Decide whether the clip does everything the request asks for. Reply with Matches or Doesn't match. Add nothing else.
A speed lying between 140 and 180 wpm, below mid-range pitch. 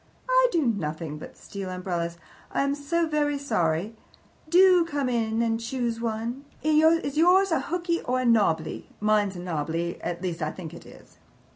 Doesn't match